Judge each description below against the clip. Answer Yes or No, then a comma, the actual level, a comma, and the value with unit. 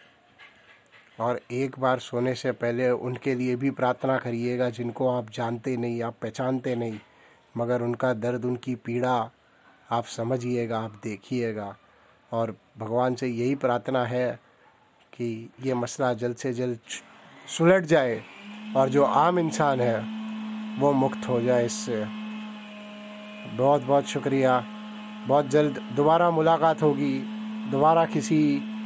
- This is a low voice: Yes, low, 130 Hz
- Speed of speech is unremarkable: Yes, average, 125 wpm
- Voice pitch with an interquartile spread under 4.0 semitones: No, average, 5.0 semitones